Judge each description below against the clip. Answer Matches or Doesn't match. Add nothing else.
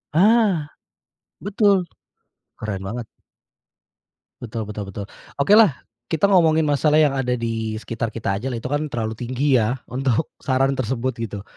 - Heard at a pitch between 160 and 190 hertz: Doesn't match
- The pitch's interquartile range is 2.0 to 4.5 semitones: Doesn't match